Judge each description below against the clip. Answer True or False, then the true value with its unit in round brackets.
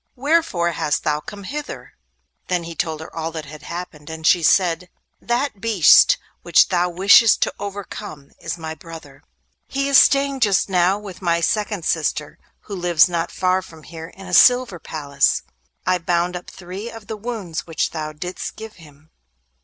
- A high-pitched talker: False (180 Hz)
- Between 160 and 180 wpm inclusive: True (175 wpm)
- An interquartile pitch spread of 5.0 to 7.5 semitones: False (4.2 semitones)